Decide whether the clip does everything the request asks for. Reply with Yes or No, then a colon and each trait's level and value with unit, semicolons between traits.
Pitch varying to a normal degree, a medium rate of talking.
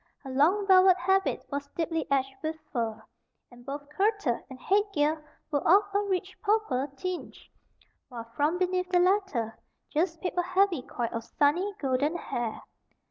No: wide, 5.7 semitones; average, 160 wpm